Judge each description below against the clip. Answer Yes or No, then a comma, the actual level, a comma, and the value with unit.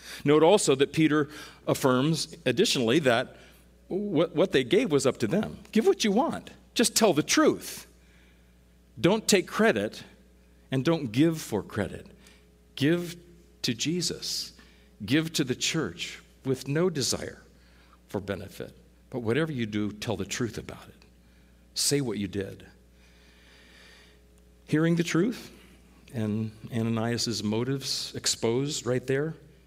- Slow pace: Yes, slow, 130 wpm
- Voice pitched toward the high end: No, low, 120 Hz